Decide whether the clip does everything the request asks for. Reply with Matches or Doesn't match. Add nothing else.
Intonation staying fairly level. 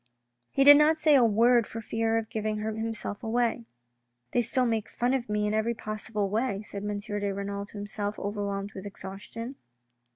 Matches